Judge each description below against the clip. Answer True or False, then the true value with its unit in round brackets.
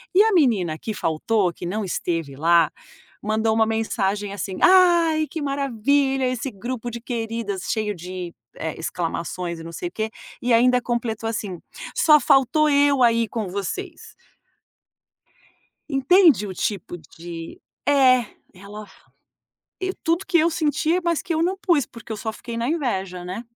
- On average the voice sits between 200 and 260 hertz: True (230 Hz)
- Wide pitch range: True (7.0 semitones)